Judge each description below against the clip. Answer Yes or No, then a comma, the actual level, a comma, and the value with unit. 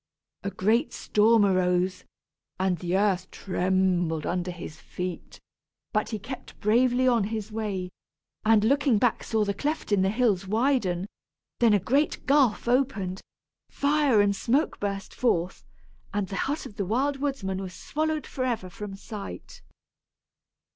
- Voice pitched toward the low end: No, high, 210 Hz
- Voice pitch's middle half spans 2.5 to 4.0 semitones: No, average, 4.8 semitones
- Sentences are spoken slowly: No, average, 145 wpm